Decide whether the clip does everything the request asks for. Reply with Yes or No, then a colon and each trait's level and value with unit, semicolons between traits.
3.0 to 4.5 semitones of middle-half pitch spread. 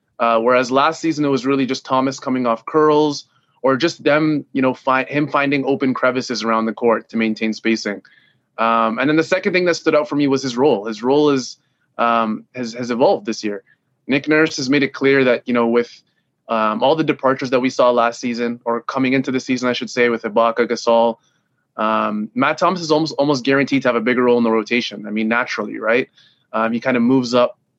Yes: average, 3.3 semitones